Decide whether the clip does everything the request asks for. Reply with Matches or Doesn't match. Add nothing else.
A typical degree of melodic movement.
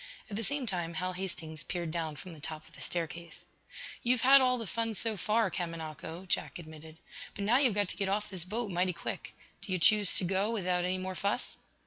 Matches